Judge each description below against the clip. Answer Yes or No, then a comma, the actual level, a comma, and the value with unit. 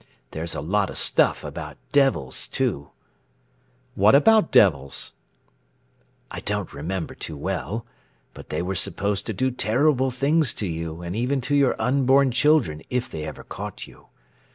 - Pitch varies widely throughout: Yes, wide, 8.1 semitones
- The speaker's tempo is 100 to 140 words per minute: No, average, 155 wpm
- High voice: No, low, 110 Hz